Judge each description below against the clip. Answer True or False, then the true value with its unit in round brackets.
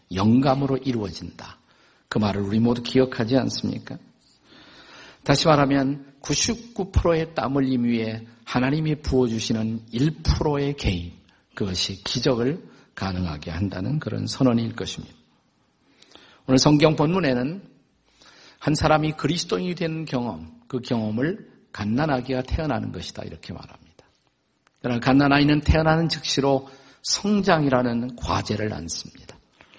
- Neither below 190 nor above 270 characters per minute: False (280 characters per minute)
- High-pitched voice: False (130 Hz)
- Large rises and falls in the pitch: False (5.0 semitones)